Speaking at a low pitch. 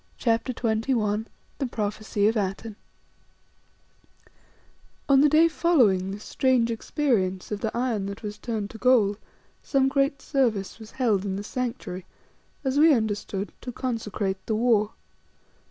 No: high, 225 Hz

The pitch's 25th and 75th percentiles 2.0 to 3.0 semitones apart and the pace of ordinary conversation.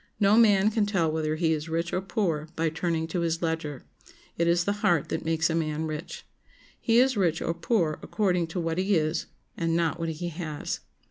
No: narrow, 2.6 semitones; fast, 210 wpm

